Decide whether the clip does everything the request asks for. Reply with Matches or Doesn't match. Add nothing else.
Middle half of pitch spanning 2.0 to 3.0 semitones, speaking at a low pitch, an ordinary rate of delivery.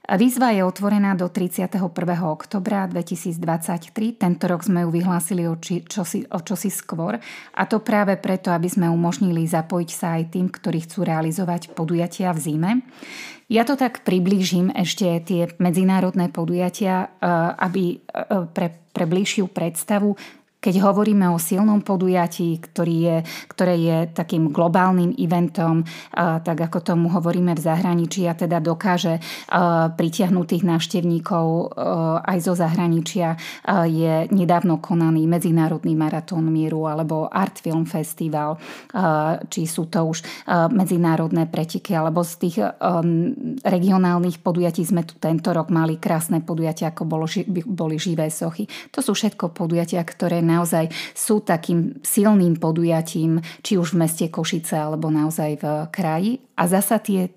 Doesn't match